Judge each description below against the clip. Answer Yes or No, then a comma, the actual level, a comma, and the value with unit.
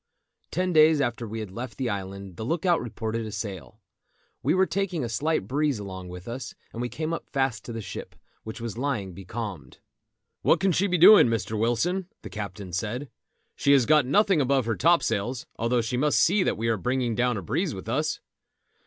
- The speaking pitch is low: Yes, low, 120 Hz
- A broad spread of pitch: Yes, wide, 6.0 semitones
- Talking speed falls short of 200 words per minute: No, fast, 205 wpm